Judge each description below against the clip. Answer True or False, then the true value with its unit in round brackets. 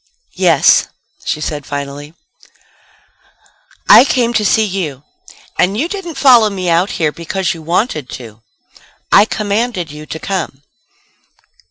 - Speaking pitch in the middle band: True (180 Hz)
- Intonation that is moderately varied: False (6.4 semitones)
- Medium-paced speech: False (130 wpm)